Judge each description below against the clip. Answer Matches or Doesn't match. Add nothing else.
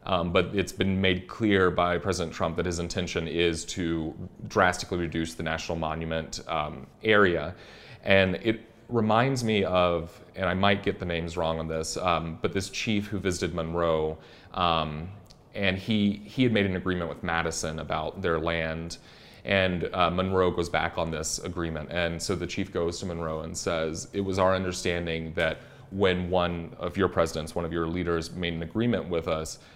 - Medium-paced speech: Matches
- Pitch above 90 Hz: Doesn't match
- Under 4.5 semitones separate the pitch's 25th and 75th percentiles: Matches